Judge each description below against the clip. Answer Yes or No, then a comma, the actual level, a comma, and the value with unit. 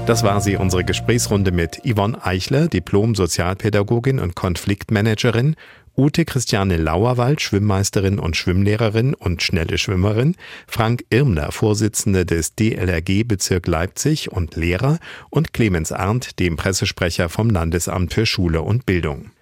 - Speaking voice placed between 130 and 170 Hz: No, low, 100 Hz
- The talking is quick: No, slow, 125 wpm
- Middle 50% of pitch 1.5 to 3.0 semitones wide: No, average, 4.2 semitones